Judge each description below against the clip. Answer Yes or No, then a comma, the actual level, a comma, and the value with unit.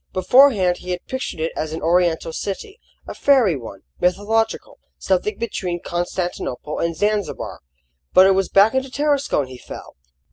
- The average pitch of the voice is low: No, medium, 185 Hz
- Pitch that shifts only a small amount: No, average, 5.3 semitones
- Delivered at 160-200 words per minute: No, average, 150 wpm